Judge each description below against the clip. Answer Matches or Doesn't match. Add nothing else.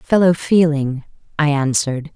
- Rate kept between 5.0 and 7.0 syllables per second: Doesn't match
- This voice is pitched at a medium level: Matches